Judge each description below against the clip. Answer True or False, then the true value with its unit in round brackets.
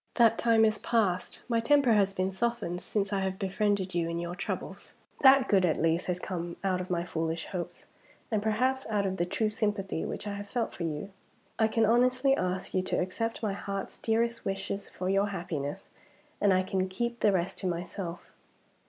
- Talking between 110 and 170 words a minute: False (200 wpm)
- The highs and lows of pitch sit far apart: False (3.6 semitones)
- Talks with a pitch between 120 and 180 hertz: False (195 Hz)